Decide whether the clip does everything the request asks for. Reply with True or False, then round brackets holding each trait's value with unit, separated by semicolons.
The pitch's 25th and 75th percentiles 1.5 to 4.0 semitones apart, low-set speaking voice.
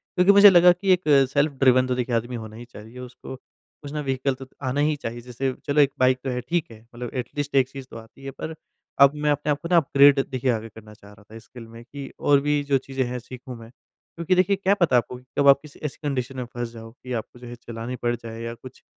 True (3.3 semitones; 130 Hz)